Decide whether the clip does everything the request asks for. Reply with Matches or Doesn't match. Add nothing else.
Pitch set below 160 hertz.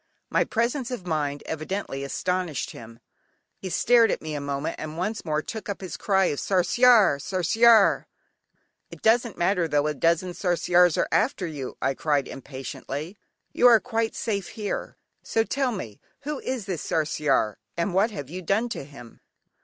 Doesn't match